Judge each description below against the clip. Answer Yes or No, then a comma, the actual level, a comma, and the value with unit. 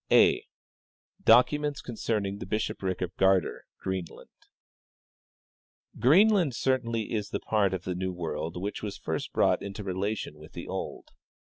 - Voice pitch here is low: Yes, low, 100 Hz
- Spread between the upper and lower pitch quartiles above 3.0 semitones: Yes, average, 3.9 semitones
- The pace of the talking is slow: No, average, 145 wpm